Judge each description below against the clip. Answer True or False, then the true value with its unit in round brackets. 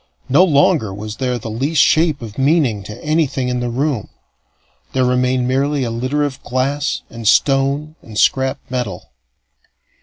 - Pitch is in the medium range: False (130 Hz)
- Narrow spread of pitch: False (3.3 semitones)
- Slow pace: False (155 wpm)